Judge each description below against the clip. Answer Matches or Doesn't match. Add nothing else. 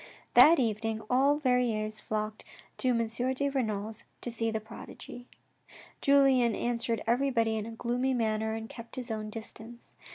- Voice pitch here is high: Matches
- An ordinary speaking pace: Matches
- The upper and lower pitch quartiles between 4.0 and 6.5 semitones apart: Doesn't match